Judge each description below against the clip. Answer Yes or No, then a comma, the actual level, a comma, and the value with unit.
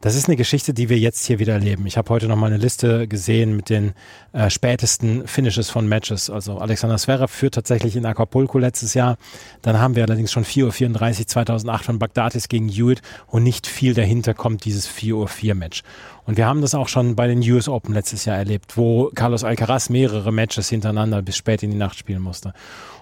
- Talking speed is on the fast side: Yes, fast, 210 wpm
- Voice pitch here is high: No, low, 115 Hz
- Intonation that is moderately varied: No, narrow, 2.2 semitones